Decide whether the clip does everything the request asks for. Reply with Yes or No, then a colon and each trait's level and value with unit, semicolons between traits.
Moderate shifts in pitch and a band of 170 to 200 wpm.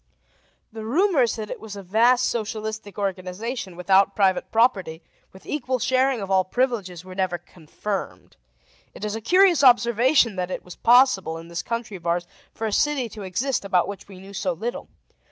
Yes: average, 4.5 semitones; average, 180 wpm